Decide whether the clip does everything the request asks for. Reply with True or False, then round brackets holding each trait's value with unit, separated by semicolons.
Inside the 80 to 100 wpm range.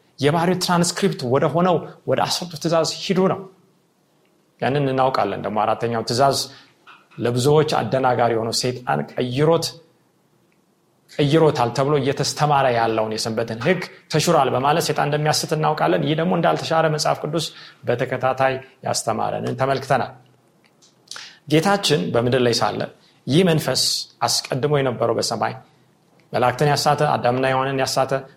False (110 wpm)